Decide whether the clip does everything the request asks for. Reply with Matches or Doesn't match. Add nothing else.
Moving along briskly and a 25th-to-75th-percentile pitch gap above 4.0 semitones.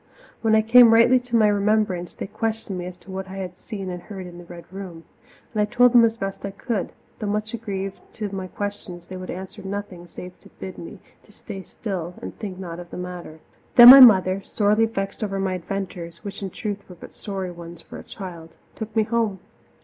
Doesn't match